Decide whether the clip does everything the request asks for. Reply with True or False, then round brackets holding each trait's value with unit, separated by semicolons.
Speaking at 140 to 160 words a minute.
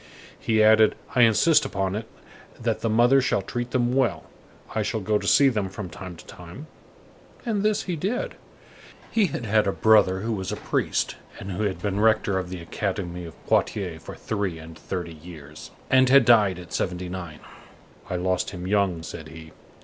False (190 wpm)